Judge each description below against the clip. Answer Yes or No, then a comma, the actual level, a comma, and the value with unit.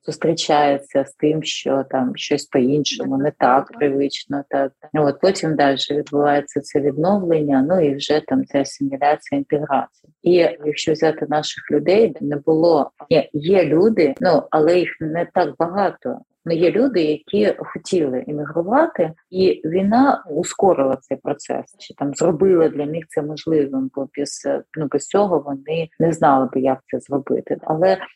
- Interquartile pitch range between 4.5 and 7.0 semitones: No, average, 2.8 semitones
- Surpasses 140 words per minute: Yes, average, 150 wpm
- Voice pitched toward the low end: No, medium, 150 Hz